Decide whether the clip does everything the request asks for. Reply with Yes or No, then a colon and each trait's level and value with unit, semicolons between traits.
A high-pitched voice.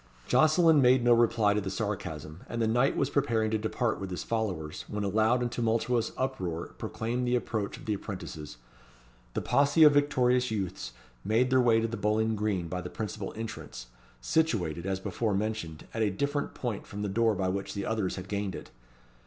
No: low, 110 Hz